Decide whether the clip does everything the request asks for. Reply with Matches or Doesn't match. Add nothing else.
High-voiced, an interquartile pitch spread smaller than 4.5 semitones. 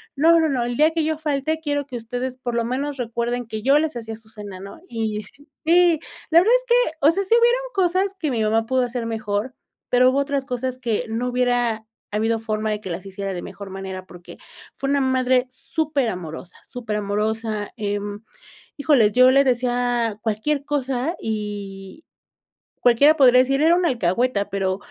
Doesn't match